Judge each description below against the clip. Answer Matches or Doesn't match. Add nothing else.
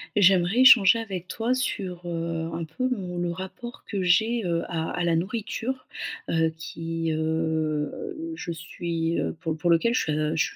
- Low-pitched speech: Doesn't match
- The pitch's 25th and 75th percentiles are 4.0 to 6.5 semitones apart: Matches